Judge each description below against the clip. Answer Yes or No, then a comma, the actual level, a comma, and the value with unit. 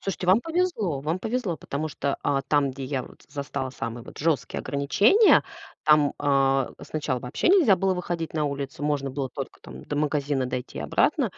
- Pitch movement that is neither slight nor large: Yes, average, 4.3 semitones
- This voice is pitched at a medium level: Yes, medium, 145 Hz